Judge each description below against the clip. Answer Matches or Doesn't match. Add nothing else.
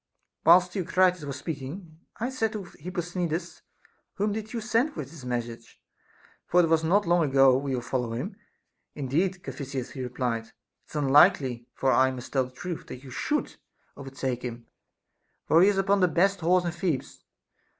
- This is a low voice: Doesn't match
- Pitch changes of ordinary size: Doesn't match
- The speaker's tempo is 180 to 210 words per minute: Matches